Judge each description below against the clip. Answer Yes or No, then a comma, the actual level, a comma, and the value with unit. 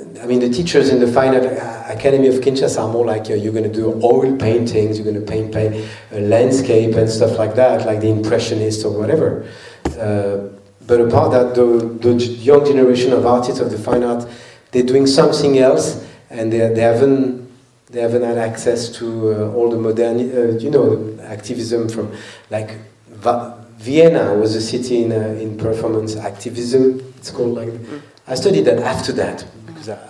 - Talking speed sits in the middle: Yes, average, 185 wpm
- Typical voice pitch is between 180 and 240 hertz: No, low, 115 Hz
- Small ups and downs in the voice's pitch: Yes, narrow, 2.2 semitones